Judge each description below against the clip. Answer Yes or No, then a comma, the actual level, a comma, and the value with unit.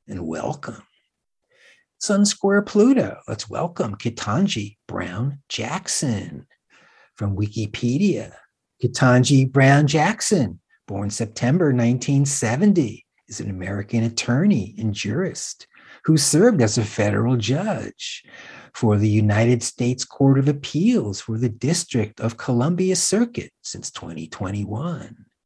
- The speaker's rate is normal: No, slow, 105 wpm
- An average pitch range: No, wide, 6.7 semitones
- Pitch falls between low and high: No, low, 125 Hz